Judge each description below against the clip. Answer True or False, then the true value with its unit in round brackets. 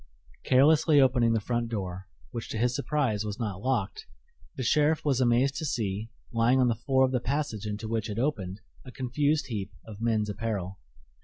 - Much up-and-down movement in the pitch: False (3.8 semitones)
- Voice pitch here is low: True (115 Hz)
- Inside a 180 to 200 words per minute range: True (185 wpm)